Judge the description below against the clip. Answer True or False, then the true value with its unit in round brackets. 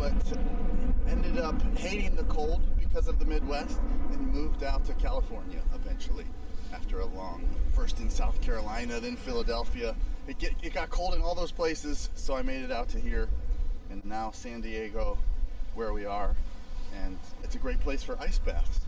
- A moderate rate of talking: True (180 wpm)